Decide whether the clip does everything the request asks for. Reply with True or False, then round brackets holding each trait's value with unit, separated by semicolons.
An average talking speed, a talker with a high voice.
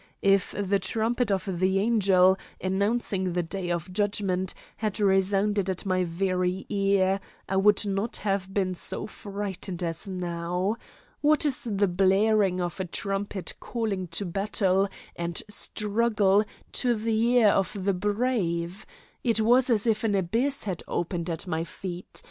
True (150 wpm; 195 Hz)